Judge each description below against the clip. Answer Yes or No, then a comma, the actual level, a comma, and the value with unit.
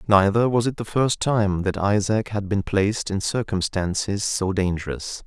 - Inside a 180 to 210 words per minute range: No, average, 170 wpm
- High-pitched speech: No, low, 100 Hz